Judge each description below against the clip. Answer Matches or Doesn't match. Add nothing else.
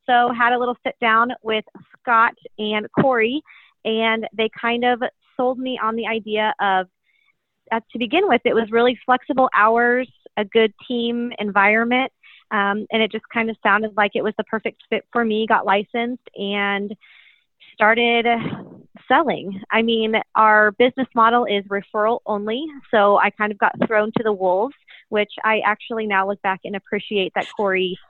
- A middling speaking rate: Matches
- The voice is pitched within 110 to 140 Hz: Doesn't match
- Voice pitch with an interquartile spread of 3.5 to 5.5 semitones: Doesn't match